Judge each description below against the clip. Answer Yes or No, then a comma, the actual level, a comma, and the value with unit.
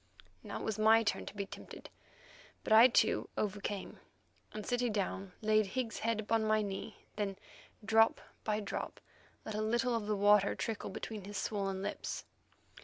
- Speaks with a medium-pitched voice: No, high, 215 Hz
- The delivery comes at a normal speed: Yes, average, 170 wpm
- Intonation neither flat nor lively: No, narrow, 1.7 semitones